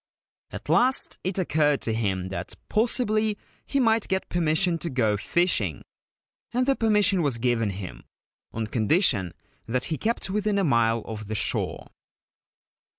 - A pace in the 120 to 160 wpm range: Yes, average, 150 wpm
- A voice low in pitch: No, medium, 155 Hz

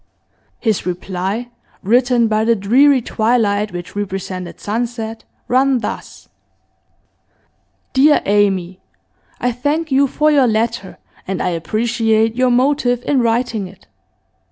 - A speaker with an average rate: No, slow, 115 wpm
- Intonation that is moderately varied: Yes, average, 3.7 semitones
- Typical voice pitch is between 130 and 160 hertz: No, high, 230 Hz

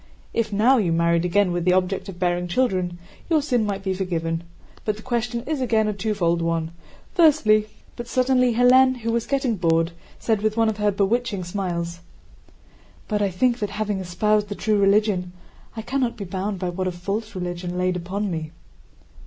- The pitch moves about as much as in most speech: Yes, average, 4.3 semitones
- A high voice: Yes, high, 205 Hz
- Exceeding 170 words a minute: Yes, average, 185 wpm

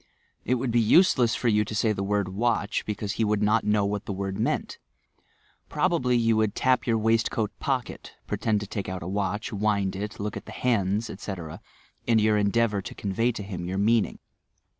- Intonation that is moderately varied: No, narrow, 2.3 semitones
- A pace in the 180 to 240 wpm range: Yes, fast, 205 wpm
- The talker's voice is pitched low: Yes, low, 105 Hz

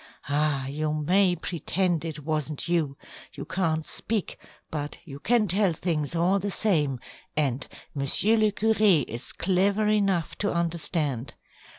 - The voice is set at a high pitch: No, medium, 165 Hz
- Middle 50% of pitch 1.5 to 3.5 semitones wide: No, average, 4.7 semitones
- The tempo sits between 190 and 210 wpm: No, slow, 135 wpm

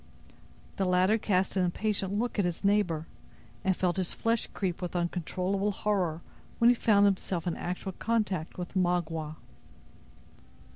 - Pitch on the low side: No, medium, 185 Hz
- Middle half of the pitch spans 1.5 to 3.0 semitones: Yes, narrow, 2.6 semitones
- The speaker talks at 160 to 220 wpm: No, average, 145 wpm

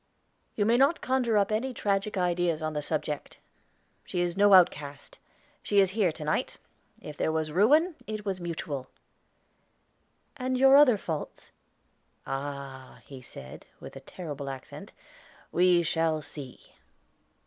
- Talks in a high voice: No, medium, 175 Hz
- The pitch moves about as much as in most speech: No, wide, 6.1 semitones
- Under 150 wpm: Yes, average, 140 wpm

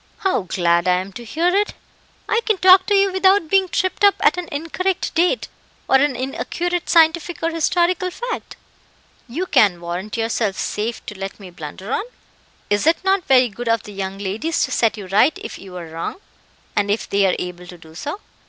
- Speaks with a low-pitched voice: No, very high, 255 Hz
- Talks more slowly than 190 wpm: No, average, 200 wpm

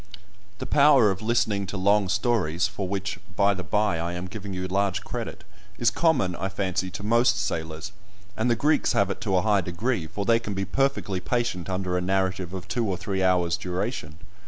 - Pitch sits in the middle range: No, very low, 95 Hz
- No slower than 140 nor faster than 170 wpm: No, fast, 205 wpm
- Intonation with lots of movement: No, average, 3.0 semitones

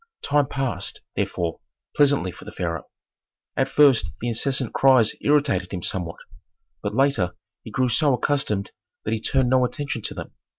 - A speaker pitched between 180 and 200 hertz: No, low, 125 Hz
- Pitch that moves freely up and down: Yes, wide, 5.8 semitones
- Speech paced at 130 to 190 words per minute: Yes, average, 160 wpm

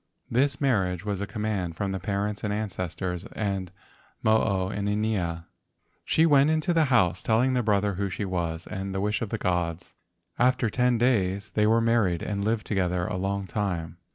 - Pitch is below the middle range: Yes, low, 100 Hz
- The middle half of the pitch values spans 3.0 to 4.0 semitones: Yes, average, 3.5 semitones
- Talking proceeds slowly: No, average, 180 wpm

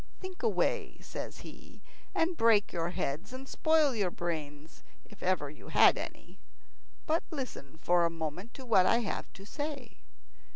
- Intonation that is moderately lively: No, wide, 8.4 semitones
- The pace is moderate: Yes, average, 160 wpm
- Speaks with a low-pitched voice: No, high, 205 Hz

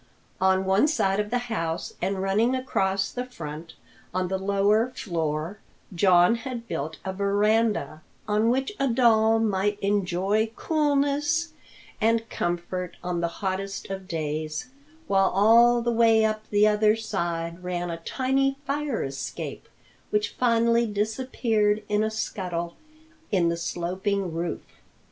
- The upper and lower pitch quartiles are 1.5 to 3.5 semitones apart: No, average, 4.2 semitones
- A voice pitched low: No, high, 205 Hz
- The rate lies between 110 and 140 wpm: Yes, slow, 135 wpm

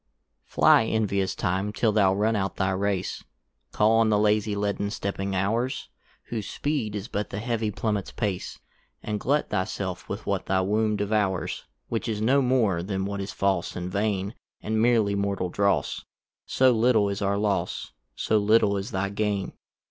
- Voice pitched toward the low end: Yes, low, 105 Hz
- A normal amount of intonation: No, narrow, 2.0 semitones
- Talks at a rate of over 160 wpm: Yes, average, 170 wpm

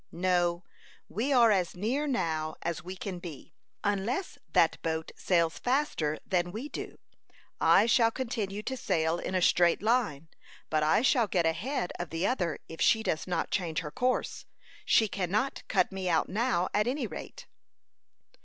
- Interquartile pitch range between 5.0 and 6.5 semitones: Yes, wide, 5.6 semitones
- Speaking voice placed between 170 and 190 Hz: Yes, medium, 185 Hz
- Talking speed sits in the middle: Yes, average, 165 wpm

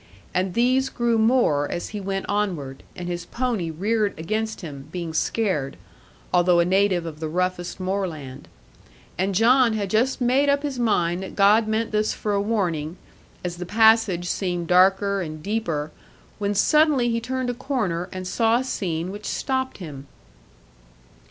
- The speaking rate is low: No, average, 165 wpm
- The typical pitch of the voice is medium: No, high, 195 Hz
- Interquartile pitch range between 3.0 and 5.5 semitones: Yes, average, 4.6 semitones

